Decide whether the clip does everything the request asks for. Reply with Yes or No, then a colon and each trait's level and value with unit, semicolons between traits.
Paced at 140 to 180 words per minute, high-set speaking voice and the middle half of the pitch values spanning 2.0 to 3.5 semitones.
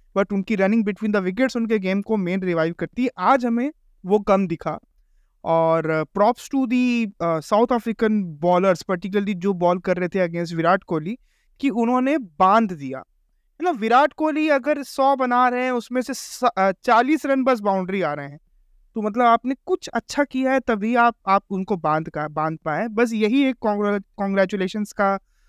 No: average, 175 wpm; high, 210 Hz; average, 5.1 semitones